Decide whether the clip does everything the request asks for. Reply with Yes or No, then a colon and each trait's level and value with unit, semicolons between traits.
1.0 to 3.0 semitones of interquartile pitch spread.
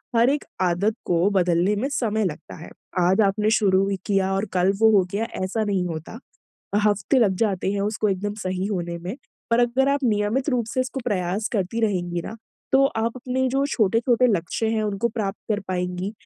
No: average, 3.6 semitones